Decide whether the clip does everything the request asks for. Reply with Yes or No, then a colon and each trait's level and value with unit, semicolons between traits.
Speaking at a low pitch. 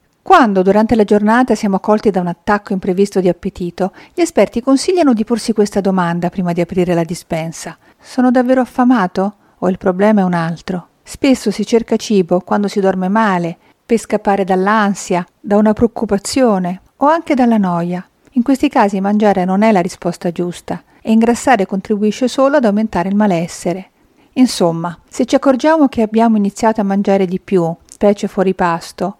No: high, 205 Hz